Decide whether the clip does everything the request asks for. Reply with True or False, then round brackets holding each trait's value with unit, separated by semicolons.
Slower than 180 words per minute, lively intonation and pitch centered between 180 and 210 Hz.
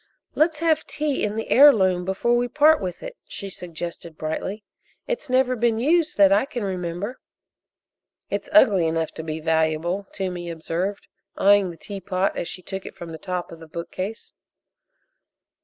True (165 wpm; 5.8 semitones; 190 Hz)